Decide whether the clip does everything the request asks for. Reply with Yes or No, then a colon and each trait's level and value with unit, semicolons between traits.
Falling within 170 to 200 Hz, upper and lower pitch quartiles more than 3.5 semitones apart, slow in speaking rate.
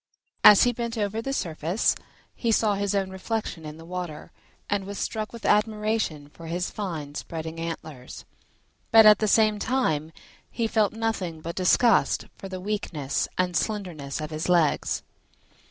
No: high, 190 Hz; average, 5.0 semitones; average, 160 wpm